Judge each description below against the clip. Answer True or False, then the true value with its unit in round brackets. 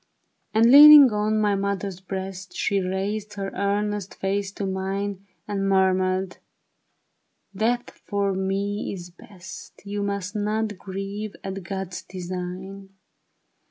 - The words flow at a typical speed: False (125 wpm)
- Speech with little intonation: True (1.4 semitones)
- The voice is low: False (195 Hz)